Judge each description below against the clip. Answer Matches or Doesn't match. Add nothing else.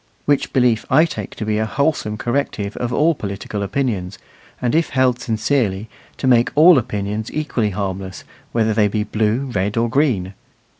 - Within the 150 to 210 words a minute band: Matches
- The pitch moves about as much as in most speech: Matches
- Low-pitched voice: Matches